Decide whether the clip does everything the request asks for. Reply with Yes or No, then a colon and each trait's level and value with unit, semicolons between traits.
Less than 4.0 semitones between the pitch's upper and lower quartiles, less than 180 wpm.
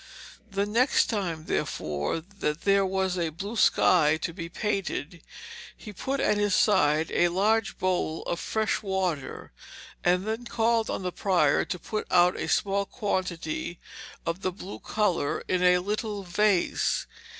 Yes: average, 3.3 semitones; average, 150 wpm